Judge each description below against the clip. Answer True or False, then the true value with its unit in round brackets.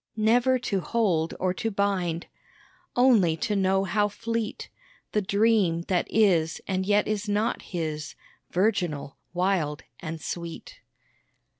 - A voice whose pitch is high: True (195 Hz)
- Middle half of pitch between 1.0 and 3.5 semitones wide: False (4.1 semitones)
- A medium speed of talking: False (125 wpm)